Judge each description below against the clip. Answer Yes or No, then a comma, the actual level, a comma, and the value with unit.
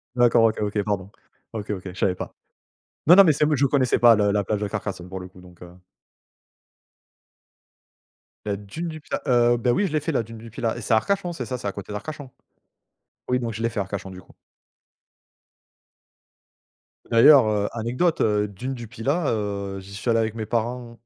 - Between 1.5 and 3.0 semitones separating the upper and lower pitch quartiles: No, average, 3.8 semitones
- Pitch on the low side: Yes, low, 115 Hz